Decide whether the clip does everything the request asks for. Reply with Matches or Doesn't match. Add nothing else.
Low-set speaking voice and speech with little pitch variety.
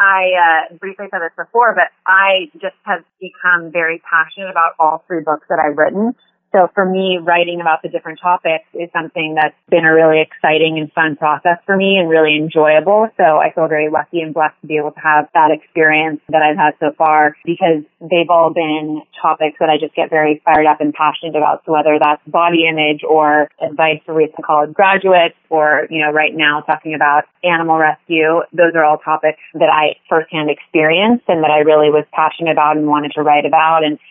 Doesn't match